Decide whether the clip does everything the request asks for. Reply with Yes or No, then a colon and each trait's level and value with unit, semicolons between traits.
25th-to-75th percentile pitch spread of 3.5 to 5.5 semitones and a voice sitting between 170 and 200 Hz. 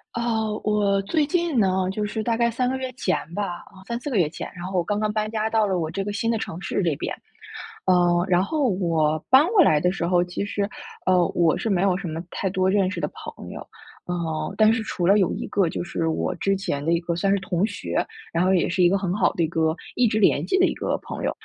Yes: average, 3.8 semitones; high, 195 Hz